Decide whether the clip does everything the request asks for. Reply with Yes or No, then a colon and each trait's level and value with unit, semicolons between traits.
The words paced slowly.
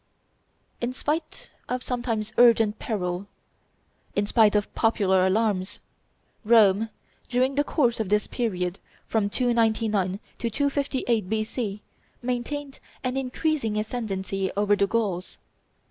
Yes: slow, 115 wpm